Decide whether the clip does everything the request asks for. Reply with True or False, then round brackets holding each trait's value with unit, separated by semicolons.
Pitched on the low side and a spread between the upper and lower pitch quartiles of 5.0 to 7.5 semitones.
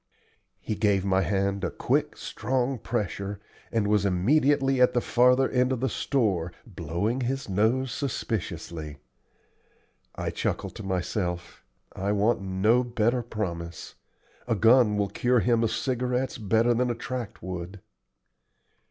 False (110 Hz; 4.5 semitones)